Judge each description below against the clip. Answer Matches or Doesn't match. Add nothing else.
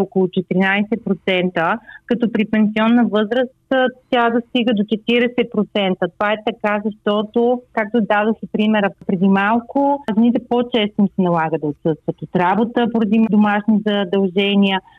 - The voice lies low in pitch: Doesn't match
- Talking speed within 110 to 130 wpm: Matches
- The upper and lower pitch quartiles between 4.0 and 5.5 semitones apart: Doesn't match